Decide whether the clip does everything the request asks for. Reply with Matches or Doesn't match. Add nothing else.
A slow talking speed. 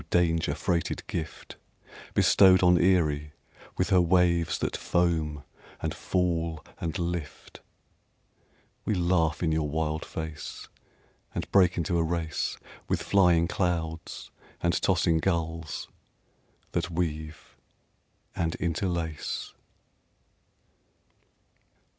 Matches